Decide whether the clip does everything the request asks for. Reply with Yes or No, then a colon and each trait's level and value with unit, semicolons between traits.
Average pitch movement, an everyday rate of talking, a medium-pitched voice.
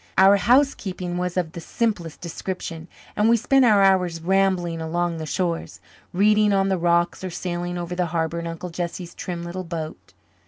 No: narrow, 2.3 semitones; average, 180 wpm; medium, 175 Hz